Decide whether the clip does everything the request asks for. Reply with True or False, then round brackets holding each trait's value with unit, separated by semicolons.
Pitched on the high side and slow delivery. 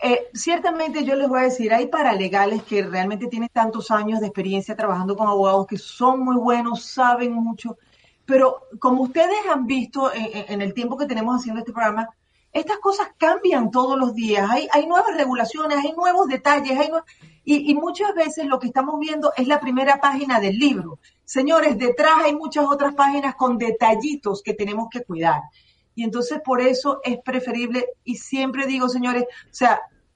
False (255 Hz; 185 wpm)